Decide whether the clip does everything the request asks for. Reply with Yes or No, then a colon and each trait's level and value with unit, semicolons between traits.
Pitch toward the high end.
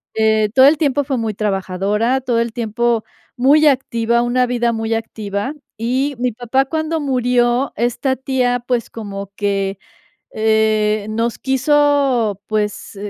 Yes: high, 235 Hz